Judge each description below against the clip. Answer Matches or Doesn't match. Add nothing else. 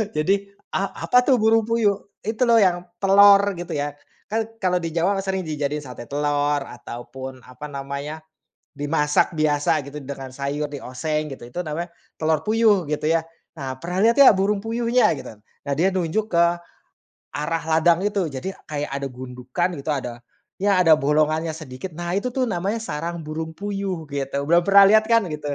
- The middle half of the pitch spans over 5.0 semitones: Matches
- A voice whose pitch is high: Doesn't match